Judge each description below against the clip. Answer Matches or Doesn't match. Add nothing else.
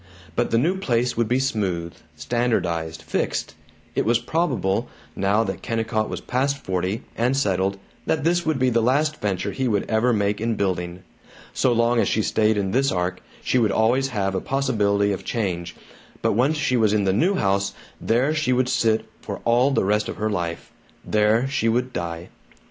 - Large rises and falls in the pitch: Doesn't match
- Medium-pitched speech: Doesn't match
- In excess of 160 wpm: Matches